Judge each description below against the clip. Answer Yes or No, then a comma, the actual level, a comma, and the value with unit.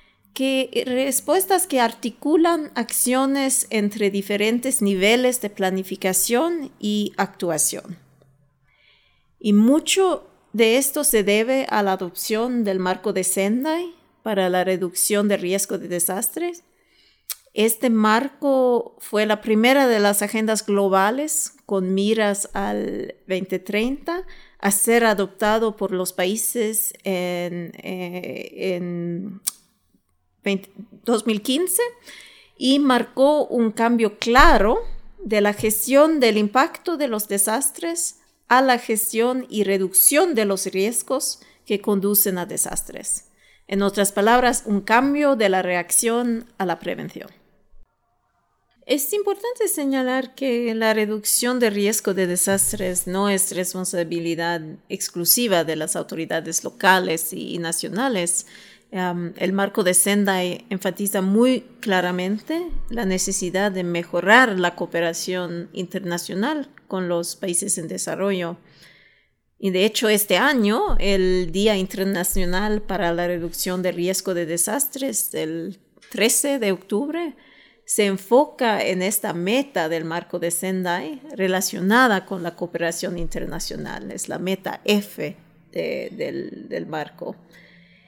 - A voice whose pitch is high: Yes, high, 205 Hz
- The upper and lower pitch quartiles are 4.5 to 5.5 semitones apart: Yes, average, 4.9 semitones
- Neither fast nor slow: No, slow, 120 wpm